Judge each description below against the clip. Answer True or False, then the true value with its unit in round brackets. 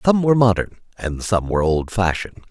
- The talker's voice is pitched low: True (100 Hz)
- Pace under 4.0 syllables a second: False (6.0 syllables/s)